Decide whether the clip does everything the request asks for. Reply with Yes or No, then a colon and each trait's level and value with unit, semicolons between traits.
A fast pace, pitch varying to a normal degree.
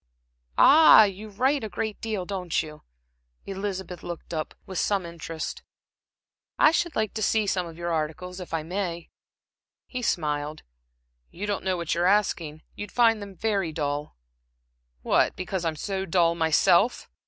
No: average, 155 wpm; average, 3.8 semitones